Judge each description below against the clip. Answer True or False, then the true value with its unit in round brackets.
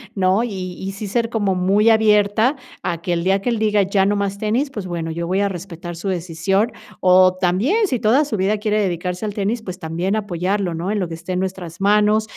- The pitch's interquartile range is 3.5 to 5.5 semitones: False (2.8 semitones)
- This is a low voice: False (195 Hz)